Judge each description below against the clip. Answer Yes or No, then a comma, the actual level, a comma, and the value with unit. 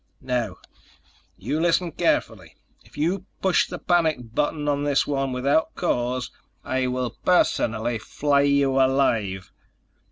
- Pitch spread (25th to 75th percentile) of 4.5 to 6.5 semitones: No, average, 3.8 semitones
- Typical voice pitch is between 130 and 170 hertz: Yes, medium, 140 Hz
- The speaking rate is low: Yes, slow, 125 wpm